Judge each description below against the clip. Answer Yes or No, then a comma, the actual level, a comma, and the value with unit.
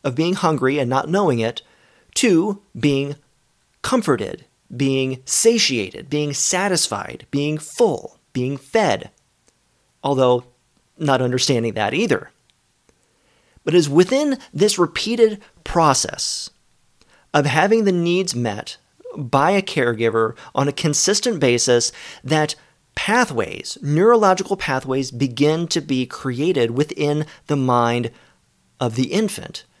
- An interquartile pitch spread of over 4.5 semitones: Yes, wide, 5.6 semitones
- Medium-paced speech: No, slow, 115 wpm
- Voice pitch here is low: No, medium, 145 Hz